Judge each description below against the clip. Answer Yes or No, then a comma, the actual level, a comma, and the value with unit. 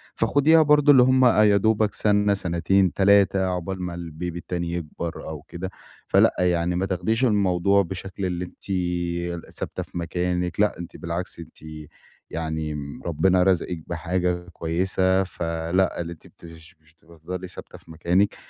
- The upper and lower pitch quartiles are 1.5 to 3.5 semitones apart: Yes, narrow, 2.4 semitones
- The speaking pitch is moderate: No, very low, 90 Hz